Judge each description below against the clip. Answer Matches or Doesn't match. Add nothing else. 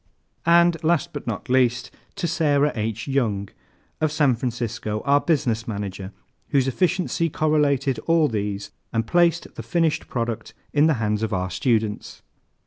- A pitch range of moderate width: Doesn't match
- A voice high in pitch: Doesn't match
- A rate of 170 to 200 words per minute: Doesn't match